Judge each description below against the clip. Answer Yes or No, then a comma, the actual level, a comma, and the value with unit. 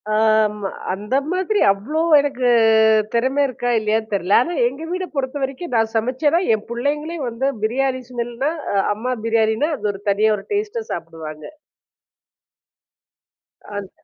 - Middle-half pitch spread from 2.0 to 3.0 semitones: No, average, 4.9 semitones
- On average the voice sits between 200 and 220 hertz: No, high, 240 Hz